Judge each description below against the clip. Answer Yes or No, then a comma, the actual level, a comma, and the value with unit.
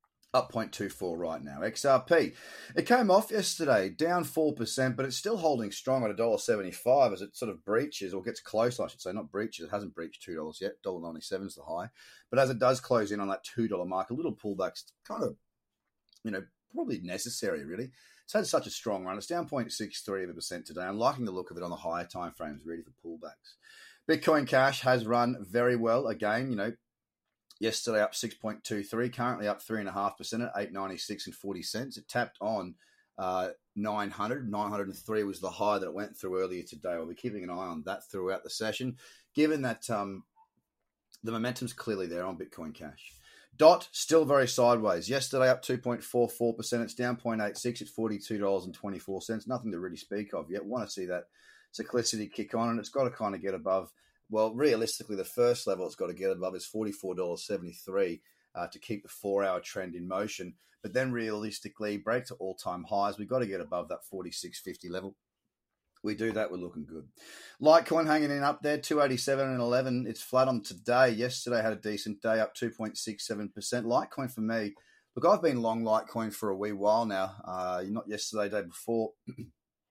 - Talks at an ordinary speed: No, fast, 210 wpm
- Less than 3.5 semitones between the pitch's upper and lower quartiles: No, average, 4.1 semitones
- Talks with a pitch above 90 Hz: Yes, low, 115 Hz